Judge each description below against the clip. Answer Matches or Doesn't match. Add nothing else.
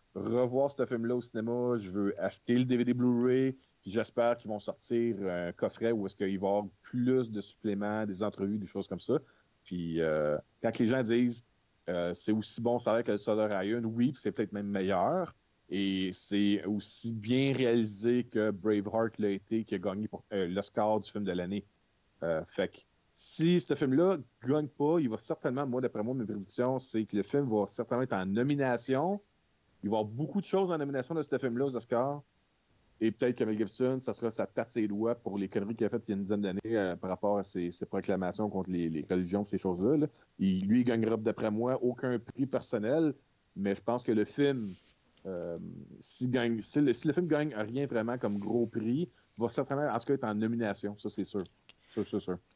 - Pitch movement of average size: Matches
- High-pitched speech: Doesn't match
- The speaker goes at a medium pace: Doesn't match